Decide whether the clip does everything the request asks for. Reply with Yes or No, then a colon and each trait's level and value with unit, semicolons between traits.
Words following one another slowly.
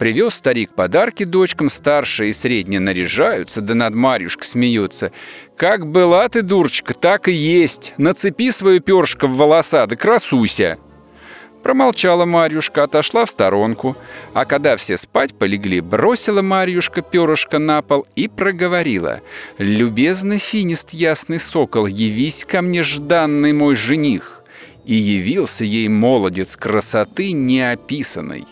No: average, 125 wpm